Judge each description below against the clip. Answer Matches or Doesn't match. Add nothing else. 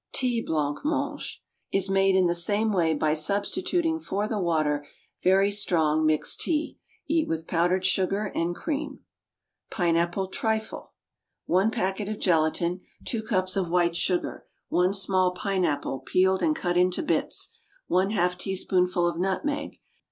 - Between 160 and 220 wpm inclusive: Doesn't match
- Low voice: Doesn't match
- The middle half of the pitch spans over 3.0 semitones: Matches